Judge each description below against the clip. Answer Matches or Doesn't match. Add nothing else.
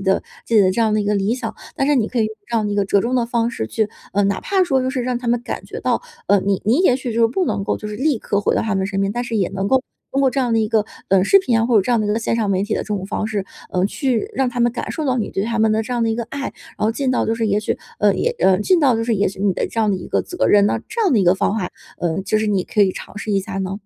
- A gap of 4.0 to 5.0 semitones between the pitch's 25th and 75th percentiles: Doesn't match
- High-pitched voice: Matches